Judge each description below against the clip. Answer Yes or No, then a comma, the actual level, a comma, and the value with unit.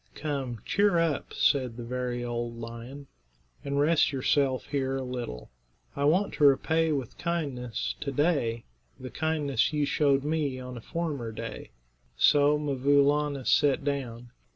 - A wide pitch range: No, average, 3.1 semitones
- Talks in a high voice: No, medium, 140 Hz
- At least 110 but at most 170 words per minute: Yes, average, 150 wpm